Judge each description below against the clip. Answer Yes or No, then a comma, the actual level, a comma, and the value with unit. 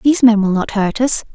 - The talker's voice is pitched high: Yes, high, 225 Hz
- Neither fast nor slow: No, fast, 270 wpm